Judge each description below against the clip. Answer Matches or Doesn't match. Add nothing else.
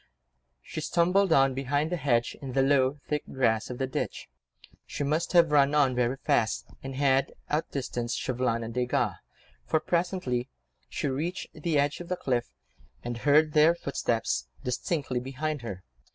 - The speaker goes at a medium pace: Matches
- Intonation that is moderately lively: Matches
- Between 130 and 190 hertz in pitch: Matches